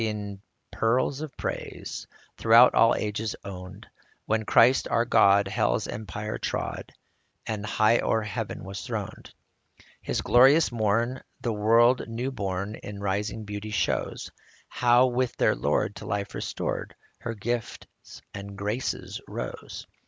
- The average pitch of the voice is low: Yes, low, 110 Hz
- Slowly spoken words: Yes, slow, 130 wpm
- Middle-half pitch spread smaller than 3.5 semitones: Yes, average, 2.8 semitones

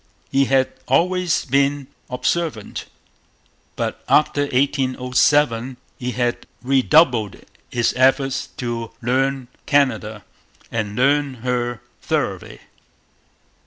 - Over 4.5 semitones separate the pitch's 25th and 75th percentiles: No, narrow, 2.5 semitones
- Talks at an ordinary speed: No, slow, 90 wpm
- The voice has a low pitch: Yes, low, 130 Hz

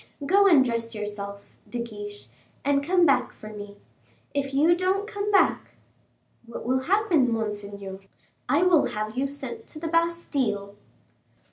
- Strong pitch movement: Yes, wide, 8.0 semitones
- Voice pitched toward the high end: Yes, very high, 260 Hz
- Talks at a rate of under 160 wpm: Yes, average, 150 wpm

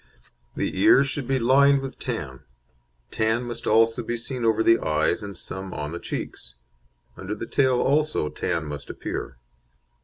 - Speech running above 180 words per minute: No, average, 160 wpm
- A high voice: No, low, 115 Hz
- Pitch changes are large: Yes, wide, 5.7 semitones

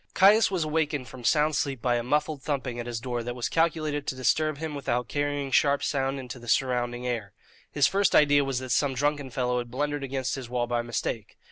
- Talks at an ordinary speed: No, fast, 220 wpm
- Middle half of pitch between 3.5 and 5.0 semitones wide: No, average, 3.1 semitones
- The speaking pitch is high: No, low, 135 Hz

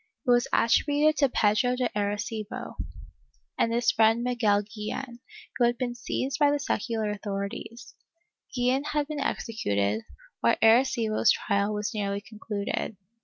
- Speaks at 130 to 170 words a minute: Yes, slow, 135 wpm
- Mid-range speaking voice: No, high, 230 Hz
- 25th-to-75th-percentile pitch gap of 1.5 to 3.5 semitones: Yes, average, 3.2 semitones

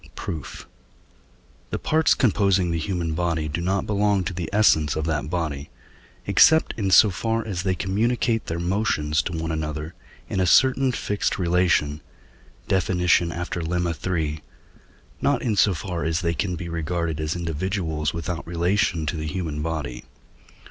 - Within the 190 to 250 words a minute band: No, average, 155 wpm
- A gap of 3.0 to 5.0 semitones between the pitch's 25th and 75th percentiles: Yes, average, 3.4 semitones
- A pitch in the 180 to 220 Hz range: No, very low, 85 Hz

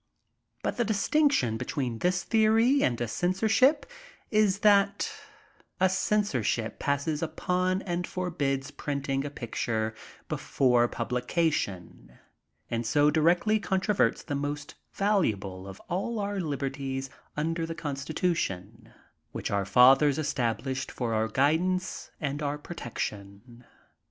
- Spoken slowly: Yes, slow, 115 wpm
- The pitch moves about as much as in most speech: No, wide, 7.1 semitones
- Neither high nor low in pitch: Yes, medium, 145 Hz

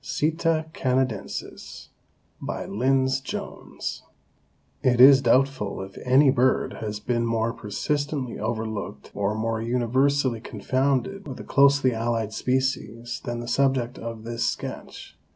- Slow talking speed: Yes, slow, 120 wpm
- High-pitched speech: No, low, 125 Hz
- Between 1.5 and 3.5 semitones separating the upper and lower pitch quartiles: Yes, average, 2.9 semitones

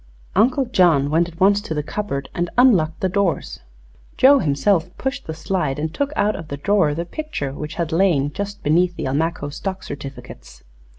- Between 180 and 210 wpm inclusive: Yes, average, 185 wpm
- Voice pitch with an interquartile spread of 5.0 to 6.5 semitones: Yes, average, 5.3 semitones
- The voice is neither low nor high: Yes, medium, 170 Hz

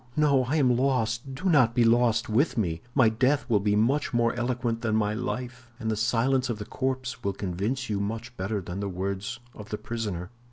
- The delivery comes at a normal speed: No, fast, 210 wpm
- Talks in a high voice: No, low, 115 Hz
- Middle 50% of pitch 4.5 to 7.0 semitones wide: No, average, 3.4 semitones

